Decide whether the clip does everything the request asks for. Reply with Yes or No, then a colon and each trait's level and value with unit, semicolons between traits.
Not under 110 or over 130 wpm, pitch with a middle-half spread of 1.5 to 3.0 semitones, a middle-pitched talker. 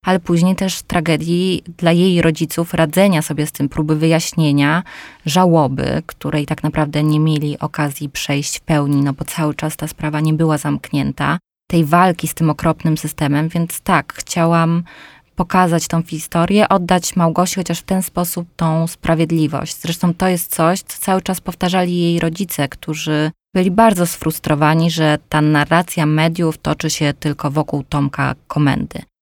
No: average, 155 wpm; narrow, 2.5 semitones; medium, 160 Hz